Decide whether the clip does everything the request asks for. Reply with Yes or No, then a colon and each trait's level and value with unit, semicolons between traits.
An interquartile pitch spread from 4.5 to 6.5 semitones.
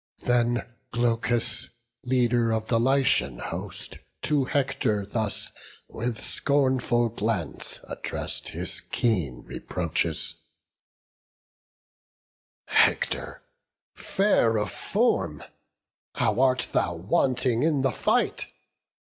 No: average, 3.5 semitones